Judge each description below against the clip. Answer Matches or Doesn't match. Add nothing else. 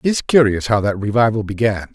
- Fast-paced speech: Matches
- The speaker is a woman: Doesn't match